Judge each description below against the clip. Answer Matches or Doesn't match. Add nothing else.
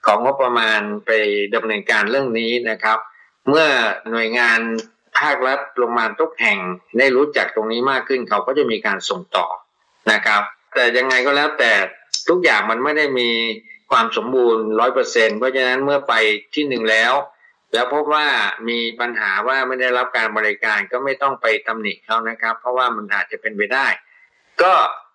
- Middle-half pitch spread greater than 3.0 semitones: Doesn't match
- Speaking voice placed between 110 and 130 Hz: Matches